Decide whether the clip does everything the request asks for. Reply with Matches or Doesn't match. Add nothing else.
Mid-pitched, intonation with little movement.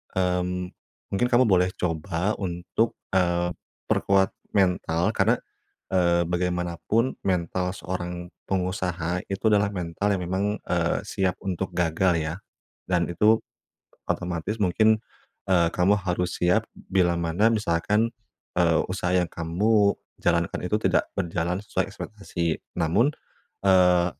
Doesn't match